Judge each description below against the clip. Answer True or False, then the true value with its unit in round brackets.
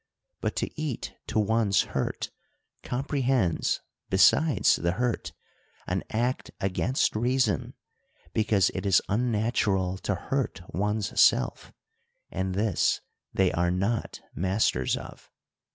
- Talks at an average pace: False (110 wpm)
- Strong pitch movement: False (4.5 semitones)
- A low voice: True (105 Hz)